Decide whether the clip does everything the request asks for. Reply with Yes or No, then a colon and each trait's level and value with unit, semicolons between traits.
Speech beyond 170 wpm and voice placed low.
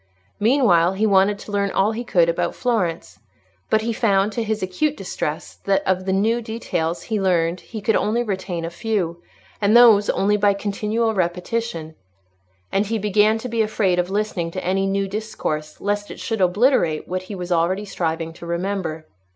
No: average, 185 wpm; high, 200 Hz